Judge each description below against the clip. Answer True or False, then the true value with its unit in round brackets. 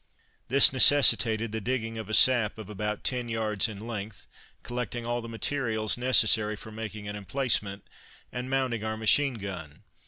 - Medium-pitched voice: False (110 Hz)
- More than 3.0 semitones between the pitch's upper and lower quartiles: False (2.6 semitones)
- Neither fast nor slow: True (160 wpm)